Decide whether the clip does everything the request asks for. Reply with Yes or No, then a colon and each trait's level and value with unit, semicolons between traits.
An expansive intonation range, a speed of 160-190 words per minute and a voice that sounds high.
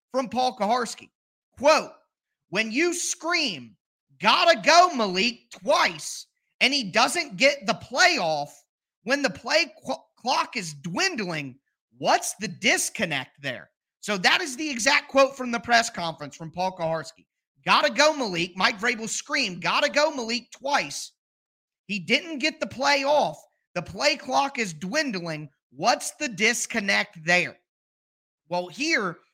No: wide, 7.9 semitones; slow, 135 wpm; high, 240 Hz